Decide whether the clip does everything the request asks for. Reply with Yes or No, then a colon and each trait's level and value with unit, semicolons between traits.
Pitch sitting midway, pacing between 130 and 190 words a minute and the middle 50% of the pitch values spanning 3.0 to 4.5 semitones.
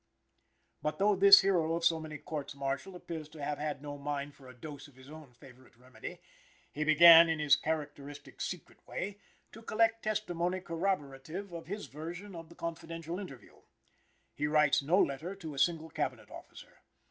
Yes: medium, 160 Hz; average, 175 wpm; average, 3.5 semitones